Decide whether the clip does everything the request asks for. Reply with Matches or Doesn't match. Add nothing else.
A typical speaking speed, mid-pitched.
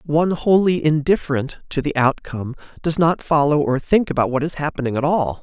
Matches